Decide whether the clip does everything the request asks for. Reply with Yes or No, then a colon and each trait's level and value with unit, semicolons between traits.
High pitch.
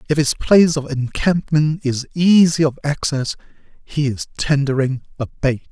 No: medium, 145 Hz